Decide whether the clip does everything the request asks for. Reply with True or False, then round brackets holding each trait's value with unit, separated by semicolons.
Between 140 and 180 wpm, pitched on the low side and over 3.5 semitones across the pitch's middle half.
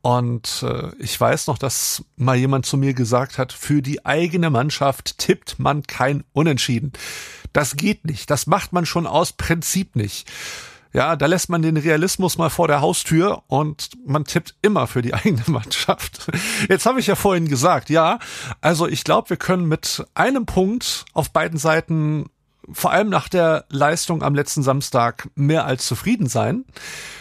False (170 wpm; 155 Hz; 4.1 semitones)